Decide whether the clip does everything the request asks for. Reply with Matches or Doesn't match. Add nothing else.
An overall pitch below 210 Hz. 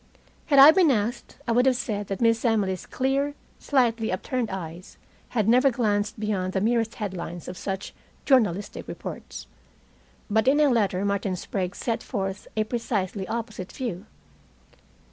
Doesn't match